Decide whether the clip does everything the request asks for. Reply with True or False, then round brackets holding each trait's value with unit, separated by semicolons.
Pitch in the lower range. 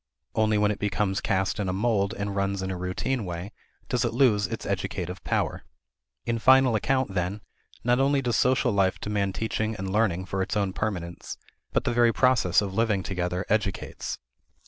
True (105 Hz)